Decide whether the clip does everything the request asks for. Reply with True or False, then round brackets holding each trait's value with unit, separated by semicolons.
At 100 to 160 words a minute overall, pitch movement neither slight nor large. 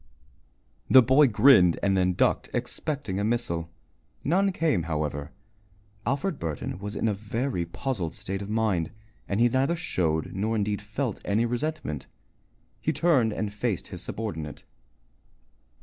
False (140 wpm; 6.4 semitones)